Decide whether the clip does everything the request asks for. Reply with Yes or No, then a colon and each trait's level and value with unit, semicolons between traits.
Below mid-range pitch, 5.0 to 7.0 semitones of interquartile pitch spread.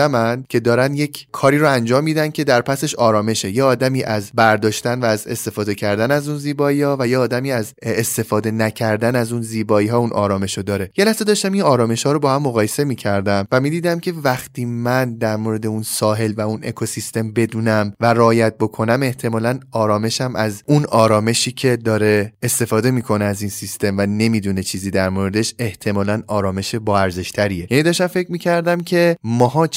No: low, 115 Hz; average, 3.7 semitones